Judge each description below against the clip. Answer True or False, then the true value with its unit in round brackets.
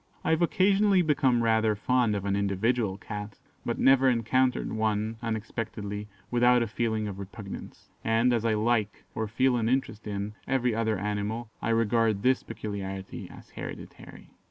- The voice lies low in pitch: True (110 Hz)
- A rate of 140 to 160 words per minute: True (155 wpm)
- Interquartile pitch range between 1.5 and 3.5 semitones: True (2.9 semitones)